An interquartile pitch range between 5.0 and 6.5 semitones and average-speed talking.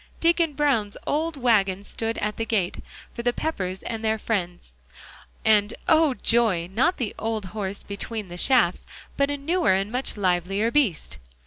Yes: average, 5.3 semitones; average, 160 wpm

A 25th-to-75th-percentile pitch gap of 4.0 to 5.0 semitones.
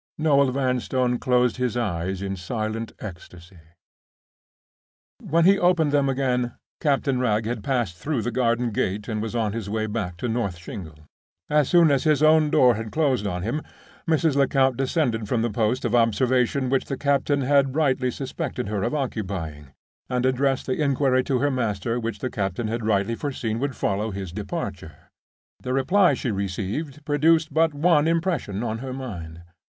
Yes: average, 4.7 semitones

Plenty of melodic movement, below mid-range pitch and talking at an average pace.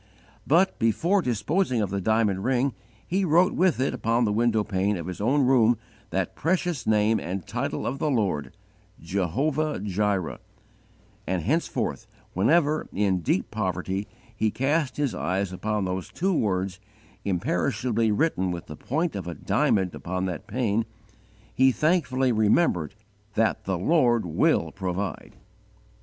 Yes: wide, 6.5 semitones; low, 110 Hz; average, 145 wpm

